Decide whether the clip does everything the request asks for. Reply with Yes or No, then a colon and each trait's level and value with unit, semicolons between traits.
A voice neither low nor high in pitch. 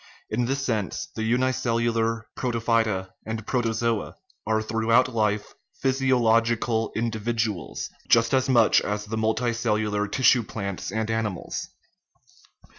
No: low, 115 Hz